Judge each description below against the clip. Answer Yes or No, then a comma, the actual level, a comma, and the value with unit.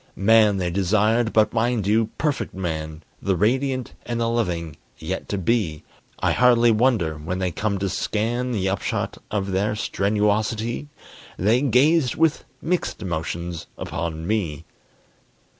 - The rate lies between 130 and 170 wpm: Yes, average, 140 wpm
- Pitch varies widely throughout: No, average, 4.6 semitones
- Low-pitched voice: Yes, low, 105 Hz